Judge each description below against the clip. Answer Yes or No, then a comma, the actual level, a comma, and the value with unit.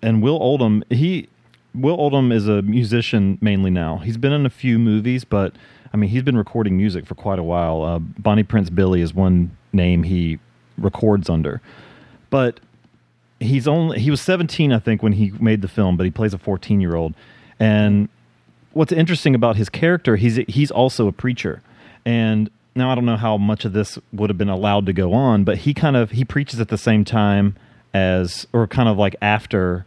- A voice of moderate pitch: No, low, 110 Hz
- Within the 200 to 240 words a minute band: Yes, fast, 205 wpm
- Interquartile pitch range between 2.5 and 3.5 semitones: No, average, 4.1 semitones